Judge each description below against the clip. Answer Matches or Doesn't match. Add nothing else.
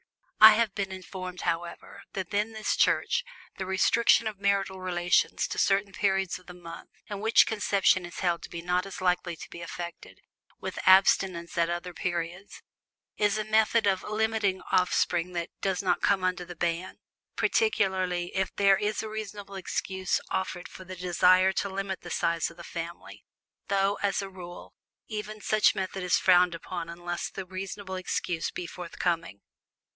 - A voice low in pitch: Doesn't match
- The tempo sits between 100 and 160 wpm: Doesn't match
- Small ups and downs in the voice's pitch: Matches